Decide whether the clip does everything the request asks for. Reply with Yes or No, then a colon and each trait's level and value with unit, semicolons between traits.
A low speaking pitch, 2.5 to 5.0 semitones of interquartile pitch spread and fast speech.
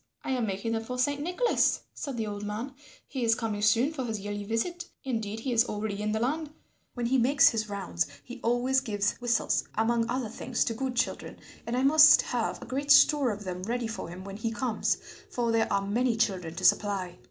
No: high, 230 Hz; average, 3.7 semitones; fast, 220 wpm